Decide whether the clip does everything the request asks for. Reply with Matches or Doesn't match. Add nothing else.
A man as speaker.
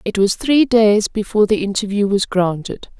Doesn't match